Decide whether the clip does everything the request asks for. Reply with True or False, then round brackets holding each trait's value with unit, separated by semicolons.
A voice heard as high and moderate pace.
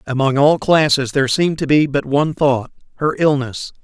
False (140 Hz; 170 wpm)